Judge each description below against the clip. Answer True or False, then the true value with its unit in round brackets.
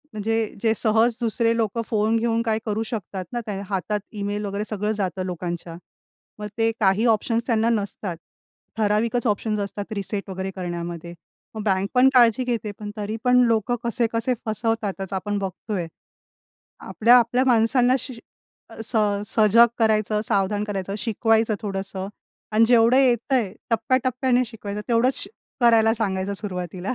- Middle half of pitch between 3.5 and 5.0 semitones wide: False (2.6 semitones)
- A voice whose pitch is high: True (215 Hz)